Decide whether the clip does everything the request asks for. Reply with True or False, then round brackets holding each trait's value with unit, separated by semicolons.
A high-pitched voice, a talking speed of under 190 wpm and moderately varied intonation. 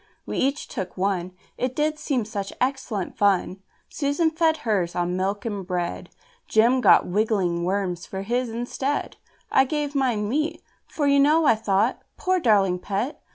False (225 Hz; 160 wpm; 6.5 semitones)